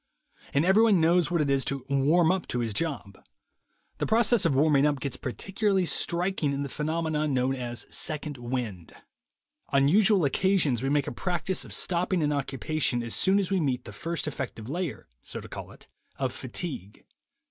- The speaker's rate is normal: Yes, average, 180 wpm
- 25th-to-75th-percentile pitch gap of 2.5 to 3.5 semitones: No, average, 5.0 semitones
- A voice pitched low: No, medium, 150 Hz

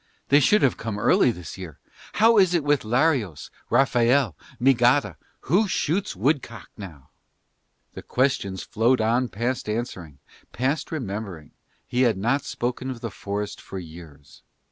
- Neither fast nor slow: Yes, average, 145 wpm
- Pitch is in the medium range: No, low, 120 Hz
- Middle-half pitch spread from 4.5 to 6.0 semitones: Yes, wide, 5.4 semitones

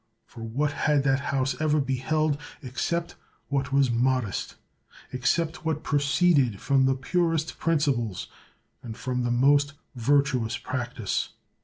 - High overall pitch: No, medium, 140 Hz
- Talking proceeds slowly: Yes, slow, 125 wpm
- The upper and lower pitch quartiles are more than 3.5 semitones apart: No, average, 2.8 semitones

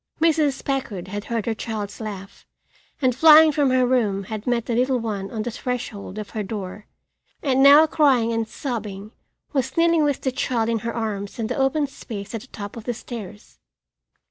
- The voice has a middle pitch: No, high, 230 Hz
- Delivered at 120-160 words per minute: No, average, 195 wpm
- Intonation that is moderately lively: Yes, average, 4.2 semitones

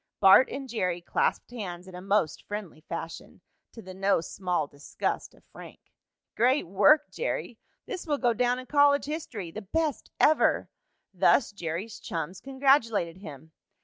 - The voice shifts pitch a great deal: Yes, wide, 6.9 semitones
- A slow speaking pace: No, average, 150 wpm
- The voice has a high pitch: Yes, high, 205 Hz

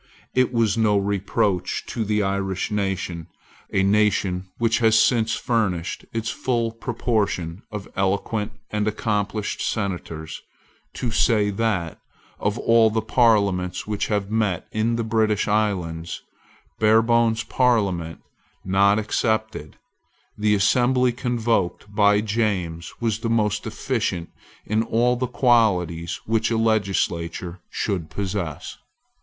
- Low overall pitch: Yes, low, 105 Hz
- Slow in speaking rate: Yes, slow, 120 wpm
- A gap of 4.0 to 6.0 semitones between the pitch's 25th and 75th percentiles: No, average, 2.8 semitones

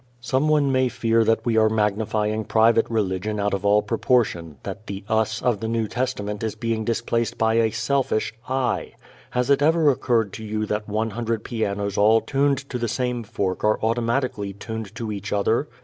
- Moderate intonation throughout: No, narrow, 2.3 semitones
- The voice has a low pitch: Yes, low, 110 Hz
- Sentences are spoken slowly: No, average, 185 wpm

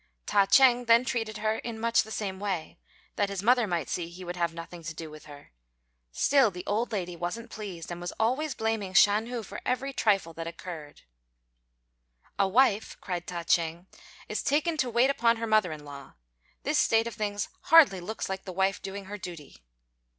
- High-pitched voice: Yes, high, 200 Hz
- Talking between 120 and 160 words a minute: No, average, 195 wpm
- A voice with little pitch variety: No, average, 4.7 semitones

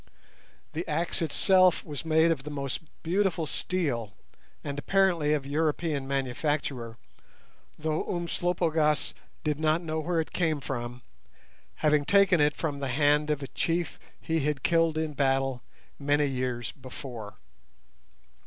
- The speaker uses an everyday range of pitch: Yes, average, 3.1 semitones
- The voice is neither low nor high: Yes, medium, 150 Hz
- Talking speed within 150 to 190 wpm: No, slow, 135 wpm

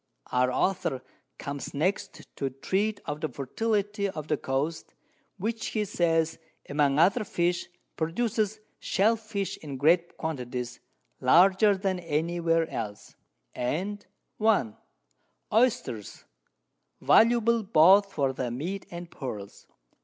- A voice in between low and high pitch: Yes, medium, 170 Hz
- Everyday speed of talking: No, slow, 115 wpm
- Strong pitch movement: Yes, wide, 6.3 semitones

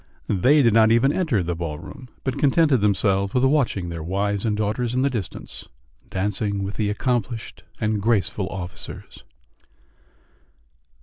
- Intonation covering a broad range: No, average, 4.2 semitones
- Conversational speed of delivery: Yes, average, 145 wpm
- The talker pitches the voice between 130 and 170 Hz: No, low, 105 Hz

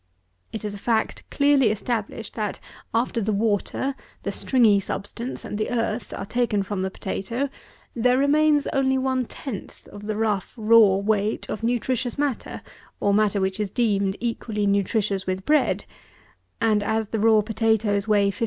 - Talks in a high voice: Yes, high, 220 Hz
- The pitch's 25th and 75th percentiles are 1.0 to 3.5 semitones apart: Yes, average, 3.0 semitones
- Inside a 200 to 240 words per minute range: No, average, 160 wpm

